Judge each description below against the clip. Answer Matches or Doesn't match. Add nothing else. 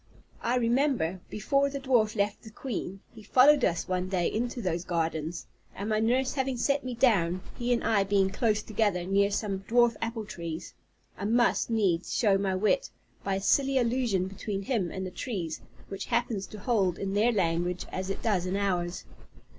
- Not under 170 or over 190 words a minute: Matches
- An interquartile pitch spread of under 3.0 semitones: Doesn't match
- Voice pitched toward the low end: Doesn't match